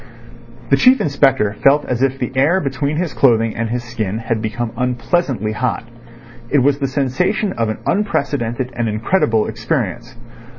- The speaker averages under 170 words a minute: Yes, average, 160 wpm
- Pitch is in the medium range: No, low, 125 Hz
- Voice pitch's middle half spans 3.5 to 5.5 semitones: Yes, average, 3.8 semitones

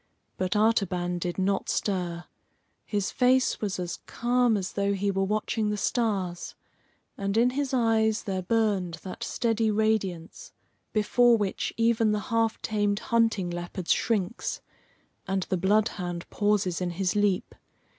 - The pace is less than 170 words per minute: Yes, average, 140 wpm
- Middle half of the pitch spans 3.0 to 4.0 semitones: Yes, average, 3.3 semitones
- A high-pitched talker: Yes, high, 205 Hz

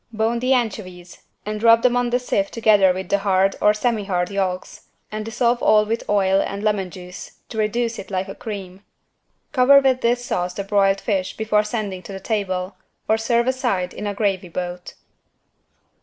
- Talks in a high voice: Yes, high, 210 Hz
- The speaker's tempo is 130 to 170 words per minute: No, average, 185 wpm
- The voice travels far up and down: No, average, 3.4 semitones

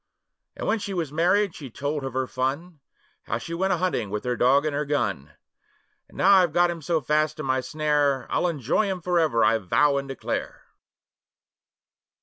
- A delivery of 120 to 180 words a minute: No, average, 190 wpm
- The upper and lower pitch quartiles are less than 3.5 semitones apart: No, average, 4.6 semitones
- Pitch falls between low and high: Yes, medium, 150 Hz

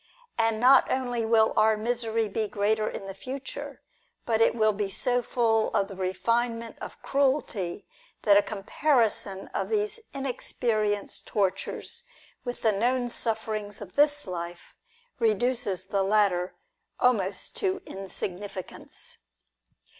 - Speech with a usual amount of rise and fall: Yes, average, 3.5 semitones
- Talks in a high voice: Yes, high, 220 Hz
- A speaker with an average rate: No, slow, 125 wpm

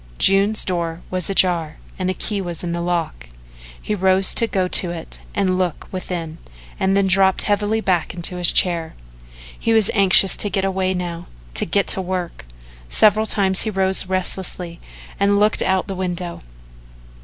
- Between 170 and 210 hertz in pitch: Yes, medium, 185 Hz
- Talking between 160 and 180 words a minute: Yes, average, 170 wpm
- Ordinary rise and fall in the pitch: No, narrow, 2.0 semitones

